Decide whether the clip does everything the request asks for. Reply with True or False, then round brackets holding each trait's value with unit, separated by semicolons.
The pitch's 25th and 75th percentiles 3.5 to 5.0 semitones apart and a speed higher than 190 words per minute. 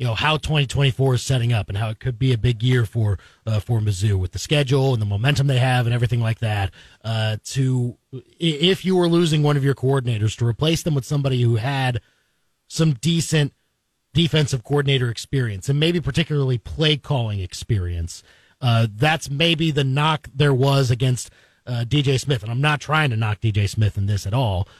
True (4.6 semitones; 200 wpm)